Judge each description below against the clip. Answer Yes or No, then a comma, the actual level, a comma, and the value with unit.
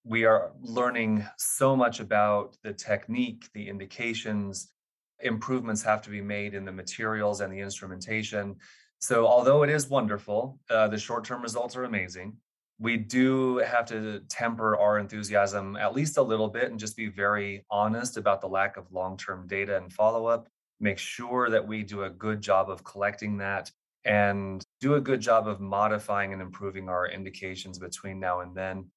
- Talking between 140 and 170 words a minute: No, average, 180 wpm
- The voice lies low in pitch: Yes, low, 105 Hz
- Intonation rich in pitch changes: No, average, 2.9 semitones